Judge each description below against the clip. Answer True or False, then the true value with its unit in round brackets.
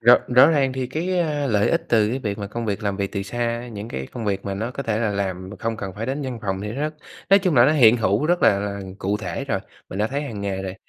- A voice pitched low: True (110 Hz)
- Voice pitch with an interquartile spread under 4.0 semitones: False (4.6 semitones)